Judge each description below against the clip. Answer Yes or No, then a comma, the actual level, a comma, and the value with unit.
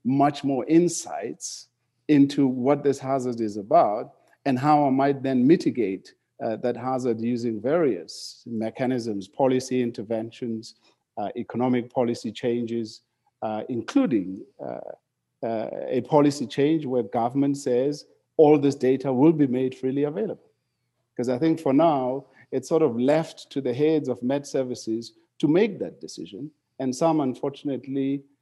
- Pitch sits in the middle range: No, low, 130 Hz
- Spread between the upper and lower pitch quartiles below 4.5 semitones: Yes, average, 2.8 semitones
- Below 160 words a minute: Yes, average, 140 wpm